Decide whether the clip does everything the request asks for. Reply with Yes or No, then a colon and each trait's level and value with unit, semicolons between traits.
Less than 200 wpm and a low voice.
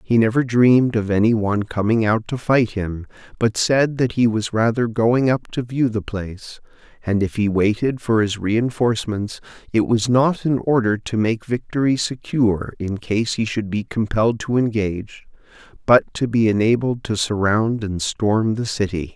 Yes: average, 180 wpm; low, 110 Hz